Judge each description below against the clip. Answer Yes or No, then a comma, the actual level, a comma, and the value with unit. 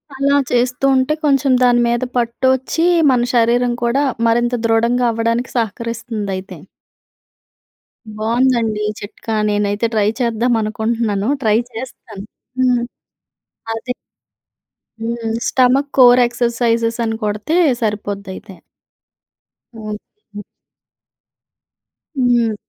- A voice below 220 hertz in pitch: No, high, 235 Hz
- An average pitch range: No, narrow, 2.2 semitones